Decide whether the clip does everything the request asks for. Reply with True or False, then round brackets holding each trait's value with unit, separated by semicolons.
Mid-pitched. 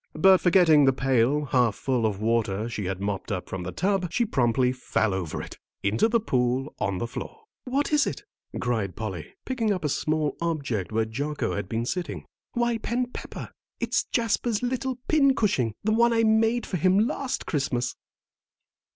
True (145 Hz)